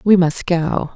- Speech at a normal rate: Yes, average, 190 wpm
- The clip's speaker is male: No, female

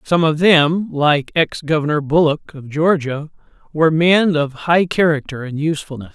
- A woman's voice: No, male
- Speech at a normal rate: Yes, average, 155 wpm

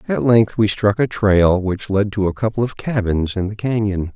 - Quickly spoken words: Yes, fast, 230 wpm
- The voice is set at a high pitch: No, low, 105 Hz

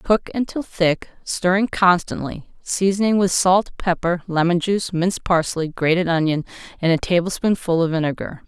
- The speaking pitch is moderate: Yes, medium, 180 Hz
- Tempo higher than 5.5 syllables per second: No, 5.0 syllables/s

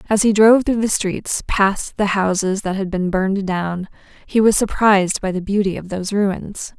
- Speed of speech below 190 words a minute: No, fast, 205 wpm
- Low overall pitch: No, high, 195 Hz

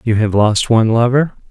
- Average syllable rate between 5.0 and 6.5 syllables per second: Yes, 5.5 syllables/s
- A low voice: Yes, low, 115 Hz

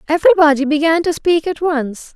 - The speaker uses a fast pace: No, average, 165 wpm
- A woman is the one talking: Yes, female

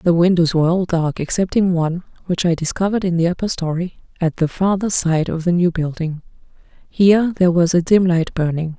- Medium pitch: Yes, medium, 175 Hz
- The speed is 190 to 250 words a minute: Yes, average, 200 wpm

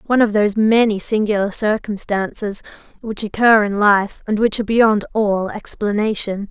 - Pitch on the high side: Yes, high, 210 Hz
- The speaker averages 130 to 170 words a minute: Yes, average, 150 wpm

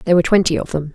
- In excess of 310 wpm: Yes, fast, 320 wpm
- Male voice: No, female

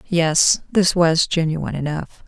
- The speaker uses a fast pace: No, slow, 130 wpm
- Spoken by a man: No, female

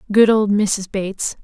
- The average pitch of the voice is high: Yes, high, 205 Hz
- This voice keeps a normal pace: Yes, average, 165 wpm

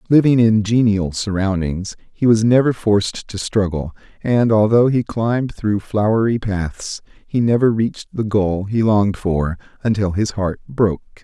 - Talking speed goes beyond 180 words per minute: No, average, 155 wpm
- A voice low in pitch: Yes, low, 105 Hz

